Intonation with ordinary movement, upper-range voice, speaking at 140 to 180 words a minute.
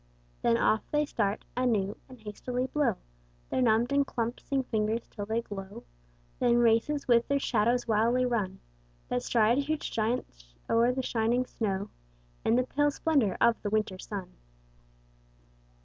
Yes: average, 3.1 semitones; high, 230 Hz; average, 150 wpm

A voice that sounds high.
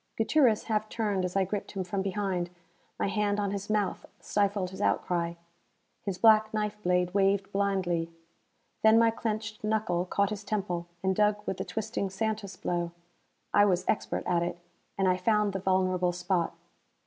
Yes: high, 195 Hz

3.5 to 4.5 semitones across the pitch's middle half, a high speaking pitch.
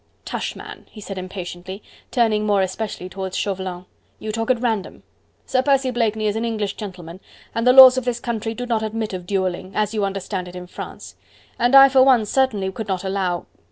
Yes: average, 3.8 semitones; high, 210 Hz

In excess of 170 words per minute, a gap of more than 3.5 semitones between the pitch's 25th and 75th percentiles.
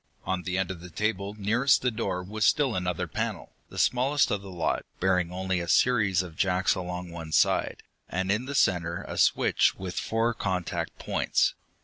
No: average, 190 wpm; average, 3.2 semitones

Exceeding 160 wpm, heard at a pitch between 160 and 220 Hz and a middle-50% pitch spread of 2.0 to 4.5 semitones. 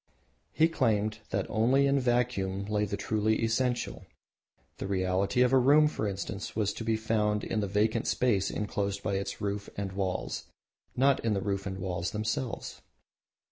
No: average, 175 wpm; low, 105 Hz; average, 3.3 semitones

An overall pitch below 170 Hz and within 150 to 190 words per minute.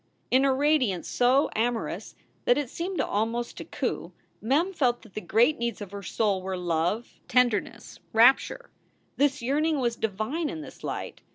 No: high, 240 Hz; average, 170 wpm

